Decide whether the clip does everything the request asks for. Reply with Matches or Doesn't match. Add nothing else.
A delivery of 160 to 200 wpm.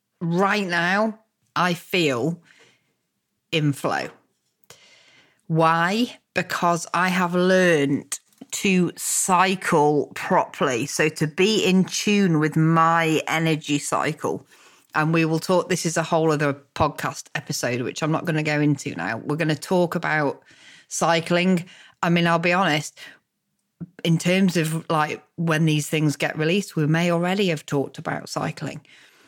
Doesn't match